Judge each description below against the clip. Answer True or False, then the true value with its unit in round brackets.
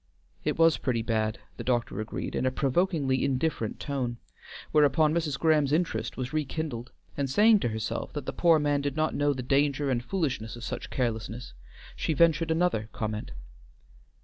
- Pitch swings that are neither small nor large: True (4.7 semitones)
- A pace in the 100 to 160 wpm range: False (170 wpm)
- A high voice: False (140 Hz)